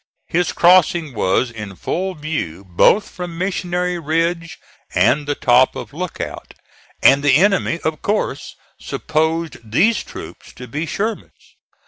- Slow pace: Yes, slow, 130 wpm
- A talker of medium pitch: Yes, medium, 165 Hz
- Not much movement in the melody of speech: No, average, 4.5 semitones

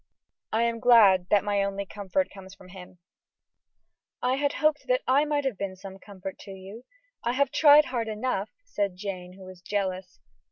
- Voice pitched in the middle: No, high, 205 Hz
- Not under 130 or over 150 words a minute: No, average, 175 wpm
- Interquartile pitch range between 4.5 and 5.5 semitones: Yes, average, 5.1 semitones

